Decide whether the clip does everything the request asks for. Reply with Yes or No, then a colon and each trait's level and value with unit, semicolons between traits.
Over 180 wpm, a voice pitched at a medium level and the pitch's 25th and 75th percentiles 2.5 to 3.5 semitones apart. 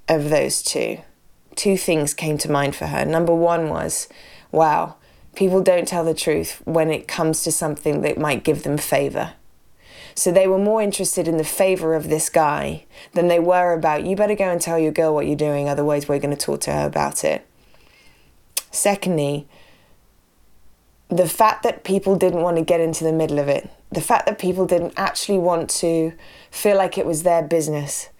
Yes: average, 195 wpm; medium, 165 Hz; average, 3.2 semitones